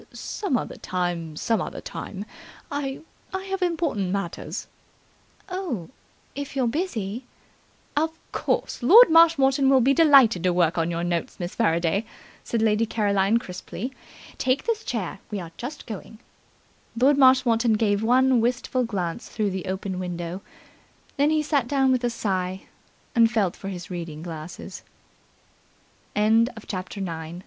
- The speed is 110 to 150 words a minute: Yes, average, 140 wpm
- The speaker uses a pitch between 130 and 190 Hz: No, high, 230 Hz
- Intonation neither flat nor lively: No, wide, 6.6 semitones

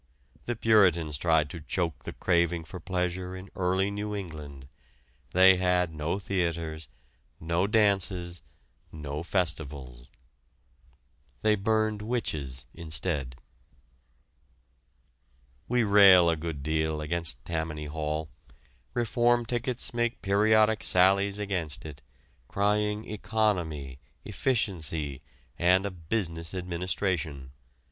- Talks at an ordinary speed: No, slow, 100 wpm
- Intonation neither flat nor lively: Yes, average, 4.4 semitones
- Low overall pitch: Yes, very low, 90 Hz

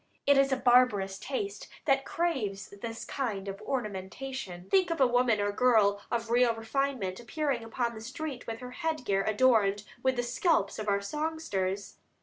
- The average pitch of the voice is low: No, high, 235 Hz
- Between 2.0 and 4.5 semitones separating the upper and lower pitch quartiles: No, average, 5.0 semitones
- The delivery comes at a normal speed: Yes, average, 170 wpm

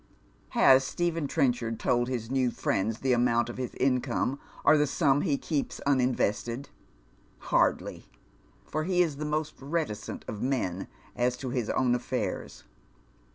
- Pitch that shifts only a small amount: No, average, 3.0 semitones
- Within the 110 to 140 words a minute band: No, average, 150 wpm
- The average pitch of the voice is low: Yes, low, 130 Hz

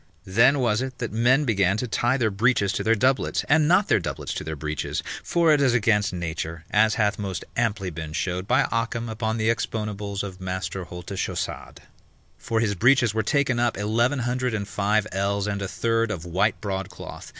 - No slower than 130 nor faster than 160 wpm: No, average, 195 wpm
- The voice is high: No, low, 110 Hz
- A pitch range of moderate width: Yes, average, 3.7 semitones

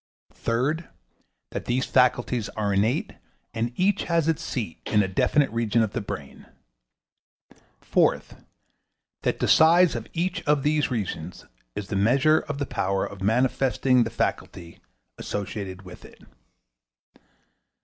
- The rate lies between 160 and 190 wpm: No, slow, 135 wpm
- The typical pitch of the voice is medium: No, low, 120 Hz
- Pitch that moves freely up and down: Yes, wide, 6.0 semitones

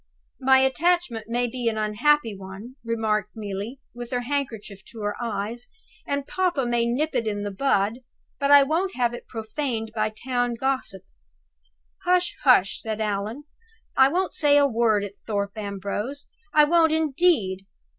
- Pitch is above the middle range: Yes, high, 240 Hz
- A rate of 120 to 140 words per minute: No, average, 160 wpm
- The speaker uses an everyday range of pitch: Yes, average, 4.9 semitones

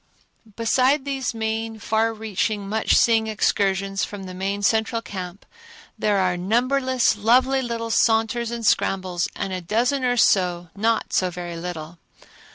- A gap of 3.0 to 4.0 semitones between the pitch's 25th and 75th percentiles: Yes, average, 3.5 semitones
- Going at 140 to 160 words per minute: Yes, average, 145 wpm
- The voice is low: No, high, 220 Hz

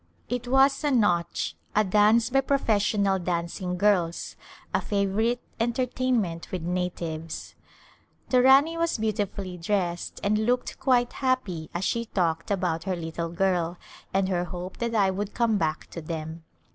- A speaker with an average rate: Yes, average, 150 wpm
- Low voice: No, high, 195 Hz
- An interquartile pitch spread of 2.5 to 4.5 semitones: No, average, 5.2 semitones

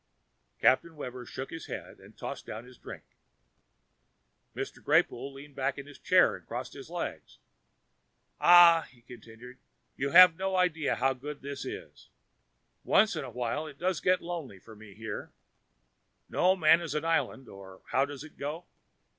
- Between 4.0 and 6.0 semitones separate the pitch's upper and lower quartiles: Yes, average, 4.7 semitones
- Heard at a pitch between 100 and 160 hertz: Yes, medium, 140 Hz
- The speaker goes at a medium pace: Yes, average, 165 wpm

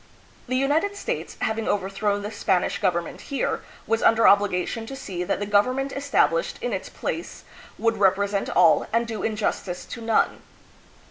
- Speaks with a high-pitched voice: Yes, high, 220 Hz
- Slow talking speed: No, average, 170 wpm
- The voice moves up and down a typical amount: Yes, average, 4.2 semitones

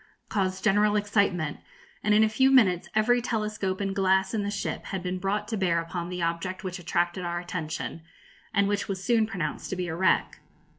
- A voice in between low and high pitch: No, high, 195 Hz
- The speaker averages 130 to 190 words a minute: No, average, 200 wpm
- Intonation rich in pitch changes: No, average, 2.9 semitones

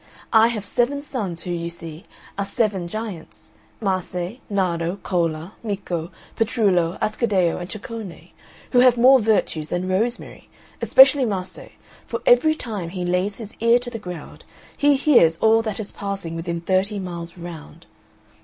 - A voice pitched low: No, high, 195 Hz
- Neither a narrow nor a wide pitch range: Yes, average, 4.7 semitones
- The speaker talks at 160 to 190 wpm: No, average, 150 wpm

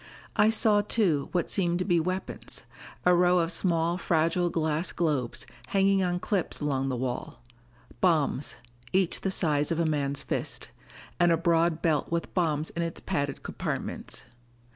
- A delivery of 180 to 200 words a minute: No, average, 160 wpm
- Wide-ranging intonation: No, average, 2.9 semitones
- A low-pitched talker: No, medium, 170 Hz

